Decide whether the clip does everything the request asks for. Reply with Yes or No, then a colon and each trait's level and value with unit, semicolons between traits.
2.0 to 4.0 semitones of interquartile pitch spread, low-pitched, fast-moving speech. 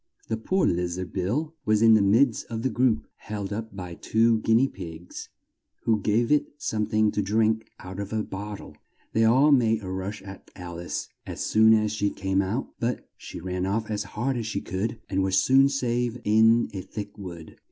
Yes: average, 3.0 semitones; low, 110 Hz; fast, 210 wpm